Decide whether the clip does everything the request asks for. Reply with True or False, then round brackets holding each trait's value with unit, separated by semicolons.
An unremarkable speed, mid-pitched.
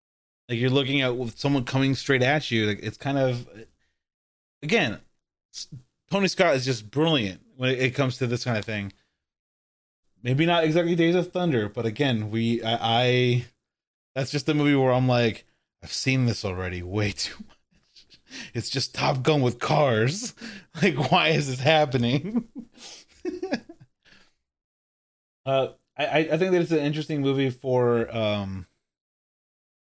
False (150 wpm; 130 Hz)